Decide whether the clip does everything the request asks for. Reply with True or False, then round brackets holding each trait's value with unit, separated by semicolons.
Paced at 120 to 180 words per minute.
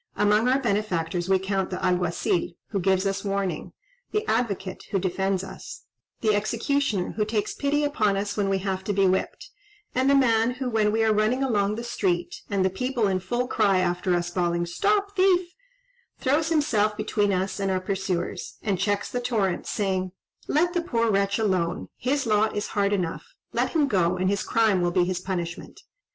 False (190 wpm)